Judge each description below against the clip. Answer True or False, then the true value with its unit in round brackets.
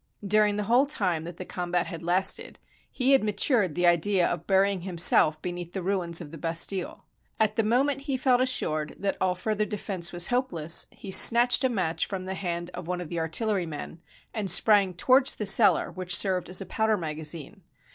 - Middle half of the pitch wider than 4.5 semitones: False (3.8 semitones)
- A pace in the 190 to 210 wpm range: True (195 wpm)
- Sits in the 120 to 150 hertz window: False (185 Hz)